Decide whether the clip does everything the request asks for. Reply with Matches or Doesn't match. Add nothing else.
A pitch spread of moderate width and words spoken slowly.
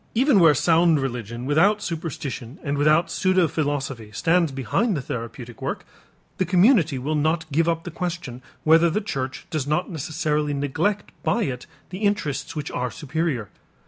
Doesn't match